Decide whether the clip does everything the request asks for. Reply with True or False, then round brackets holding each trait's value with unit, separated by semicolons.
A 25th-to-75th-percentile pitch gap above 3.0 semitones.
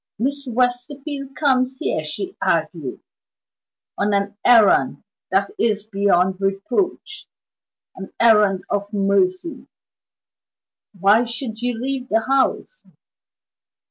True (4.9 semitones)